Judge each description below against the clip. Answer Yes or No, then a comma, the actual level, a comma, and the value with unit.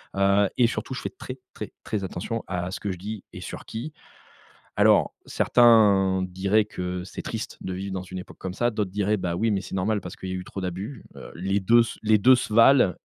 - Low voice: Yes, low, 100 Hz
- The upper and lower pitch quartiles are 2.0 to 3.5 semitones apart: Yes, average, 2.9 semitones